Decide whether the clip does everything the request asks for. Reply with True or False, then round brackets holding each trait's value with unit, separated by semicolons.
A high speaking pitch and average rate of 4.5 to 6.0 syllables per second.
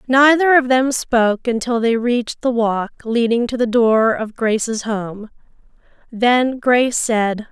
False (235 Hz; 4.0 syllables/s)